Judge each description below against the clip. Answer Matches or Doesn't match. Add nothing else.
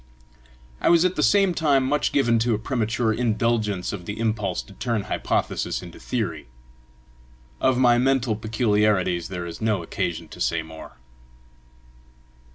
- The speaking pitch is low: Matches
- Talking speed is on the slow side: Doesn't match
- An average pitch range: Matches